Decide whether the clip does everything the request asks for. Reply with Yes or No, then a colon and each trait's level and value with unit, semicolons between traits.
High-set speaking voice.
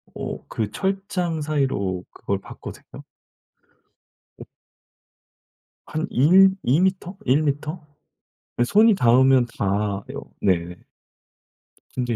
No: low, 135 Hz